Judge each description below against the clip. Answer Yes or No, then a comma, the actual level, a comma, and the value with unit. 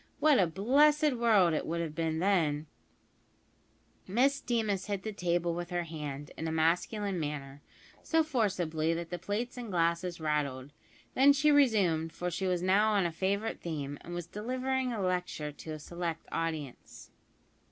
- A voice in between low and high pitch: Yes, medium, 175 Hz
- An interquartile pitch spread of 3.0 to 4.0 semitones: No, average, 5.2 semitones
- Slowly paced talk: No, average, 165 wpm